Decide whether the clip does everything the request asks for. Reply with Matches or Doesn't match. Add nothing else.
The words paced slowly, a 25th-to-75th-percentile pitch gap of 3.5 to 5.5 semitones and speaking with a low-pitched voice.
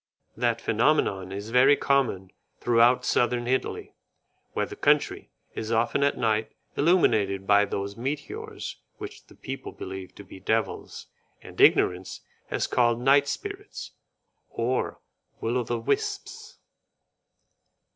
Matches